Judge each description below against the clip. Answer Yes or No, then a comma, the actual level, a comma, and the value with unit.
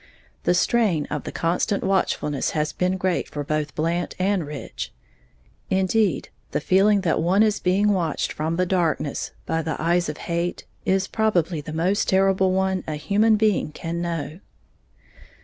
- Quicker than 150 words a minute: Yes, average, 160 wpm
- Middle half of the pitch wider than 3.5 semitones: No, average, 3.1 semitones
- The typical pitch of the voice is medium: Yes, medium, 180 Hz